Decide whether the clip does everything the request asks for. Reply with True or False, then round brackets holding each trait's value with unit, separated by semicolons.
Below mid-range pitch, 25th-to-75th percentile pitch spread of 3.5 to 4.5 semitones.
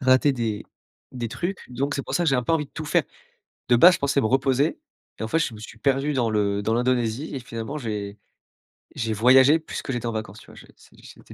True (125 Hz; 4.0 semitones)